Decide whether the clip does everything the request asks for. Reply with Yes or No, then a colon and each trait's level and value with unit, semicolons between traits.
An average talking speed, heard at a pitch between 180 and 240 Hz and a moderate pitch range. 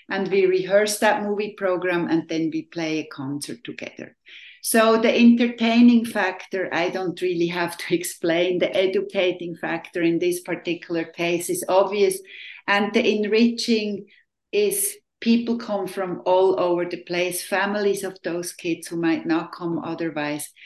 Yes: average, 150 wpm; medium, 185 Hz; average, 3.4 semitones